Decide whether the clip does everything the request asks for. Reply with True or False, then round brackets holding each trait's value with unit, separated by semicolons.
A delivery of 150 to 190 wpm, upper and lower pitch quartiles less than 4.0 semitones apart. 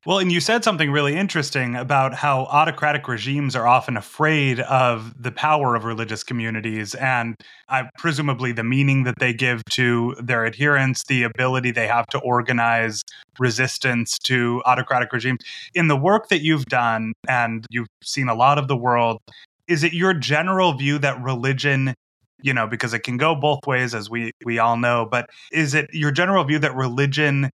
True (180 wpm; 3.4 semitones)